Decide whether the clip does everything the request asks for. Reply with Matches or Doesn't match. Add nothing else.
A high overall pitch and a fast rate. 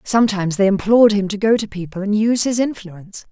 Matches